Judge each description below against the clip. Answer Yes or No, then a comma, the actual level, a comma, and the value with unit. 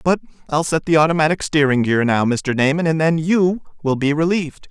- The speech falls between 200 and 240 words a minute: Yes, fast, 205 wpm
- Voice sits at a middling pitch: Yes, medium, 155 Hz